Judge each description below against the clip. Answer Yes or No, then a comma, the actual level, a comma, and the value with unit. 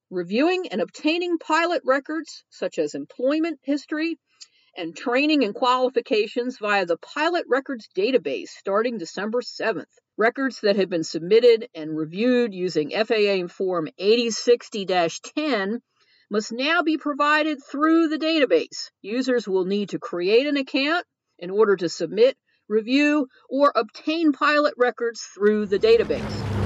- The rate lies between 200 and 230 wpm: No, slow, 135 wpm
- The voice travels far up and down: Yes, wide, 6.9 semitones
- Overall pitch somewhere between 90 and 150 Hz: No, very high, 250 Hz